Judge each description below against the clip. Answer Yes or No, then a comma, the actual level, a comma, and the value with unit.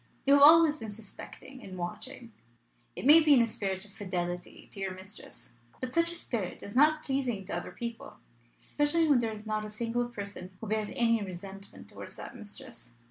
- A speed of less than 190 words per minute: No, average, 195 wpm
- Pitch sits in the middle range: No, high, 220 Hz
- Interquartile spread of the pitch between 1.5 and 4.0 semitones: No, average, 5.3 semitones